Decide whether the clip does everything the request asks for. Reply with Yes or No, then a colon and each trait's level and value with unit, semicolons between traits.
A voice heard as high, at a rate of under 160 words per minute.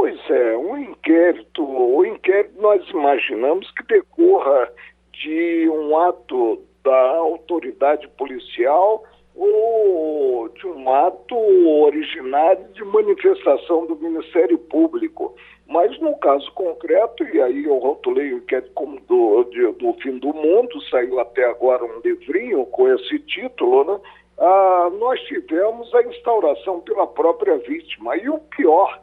Yes: very high, 340 Hz; average, 135 wpm